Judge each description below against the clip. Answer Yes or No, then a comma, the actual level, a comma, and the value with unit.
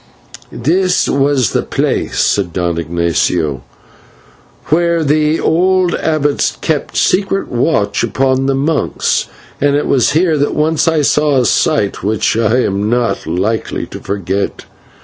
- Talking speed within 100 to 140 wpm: Yes, slow, 135 wpm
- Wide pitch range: Yes, wide, 7.5 semitones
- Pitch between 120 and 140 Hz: Yes, low, 135 Hz